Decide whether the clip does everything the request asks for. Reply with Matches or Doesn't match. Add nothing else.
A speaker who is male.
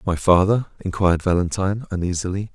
Matches